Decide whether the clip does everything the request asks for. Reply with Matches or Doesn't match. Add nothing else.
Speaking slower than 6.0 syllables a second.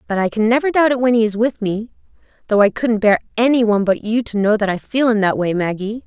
Doesn't match